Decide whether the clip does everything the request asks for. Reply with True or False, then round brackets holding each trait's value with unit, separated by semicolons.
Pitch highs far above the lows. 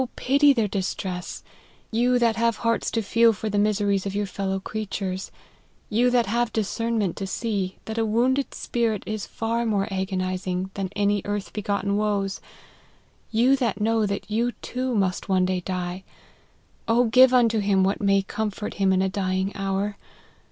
False (3.0 semitones)